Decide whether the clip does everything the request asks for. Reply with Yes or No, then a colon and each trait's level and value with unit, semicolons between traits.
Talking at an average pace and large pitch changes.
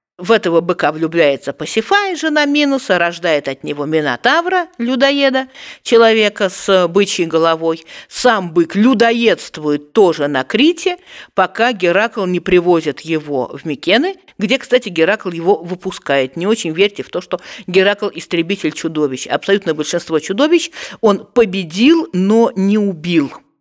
Yes: average, 130 wpm; wide, 6.6 semitones